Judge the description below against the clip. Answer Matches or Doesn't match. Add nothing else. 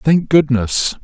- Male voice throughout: Matches